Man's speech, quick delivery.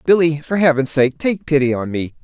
Yes: male; fast, 215 wpm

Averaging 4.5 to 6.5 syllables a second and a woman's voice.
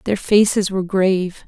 Yes: 5.2 syllables/s; female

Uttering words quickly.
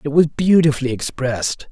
No: average, 140 wpm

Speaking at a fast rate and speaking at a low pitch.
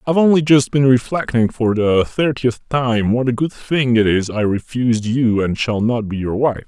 Yes: fast, 215 wpm; low, 120 Hz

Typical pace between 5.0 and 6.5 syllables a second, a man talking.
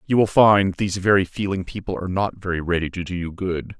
Yes: 6.0 syllables/s; male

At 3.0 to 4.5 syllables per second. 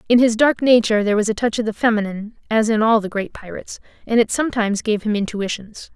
No: 6.7 syllables/s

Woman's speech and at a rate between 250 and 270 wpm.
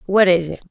Yes: female; fast, 255 wpm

